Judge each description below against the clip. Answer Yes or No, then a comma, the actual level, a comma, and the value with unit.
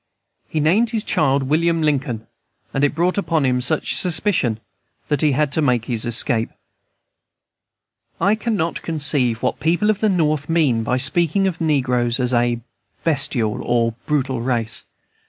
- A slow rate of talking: No, average, 155 wpm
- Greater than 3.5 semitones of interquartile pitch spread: Yes, average, 5.2 semitones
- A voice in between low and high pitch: Yes, medium, 145 Hz